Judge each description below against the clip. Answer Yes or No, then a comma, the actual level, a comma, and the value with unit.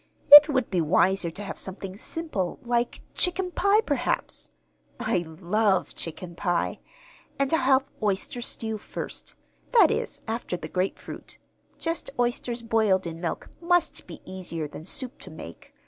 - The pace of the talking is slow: No, average, 145 wpm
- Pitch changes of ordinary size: No, wide, 6.5 semitones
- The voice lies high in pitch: Yes, high, 210 Hz